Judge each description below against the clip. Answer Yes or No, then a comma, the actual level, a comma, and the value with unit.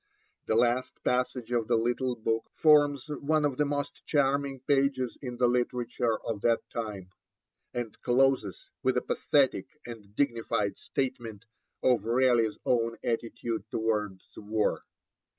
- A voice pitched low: Yes, low, 120 Hz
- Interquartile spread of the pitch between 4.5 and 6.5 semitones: No, average, 3.0 semitones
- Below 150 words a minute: Yes, slow, 135 wpm